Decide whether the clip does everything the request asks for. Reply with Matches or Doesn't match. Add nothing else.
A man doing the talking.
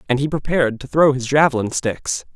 Matches